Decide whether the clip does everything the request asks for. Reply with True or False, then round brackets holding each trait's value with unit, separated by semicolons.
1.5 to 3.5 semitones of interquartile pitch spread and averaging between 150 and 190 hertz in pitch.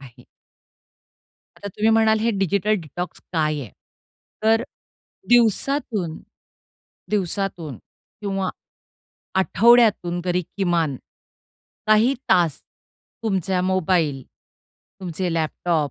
False (4.6 semitones; 185 Hz)